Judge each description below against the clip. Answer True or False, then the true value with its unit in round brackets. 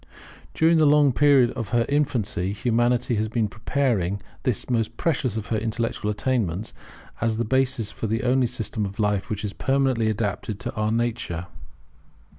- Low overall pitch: True (115 Hz)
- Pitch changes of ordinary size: True (3.2 semitones)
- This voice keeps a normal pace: True (170 wpm)